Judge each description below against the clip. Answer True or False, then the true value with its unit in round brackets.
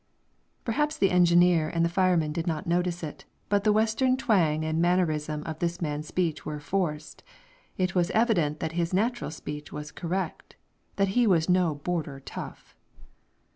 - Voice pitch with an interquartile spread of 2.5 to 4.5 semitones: True (3.4 semitones)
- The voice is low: False (175 Hz)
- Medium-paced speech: True (160 wpm)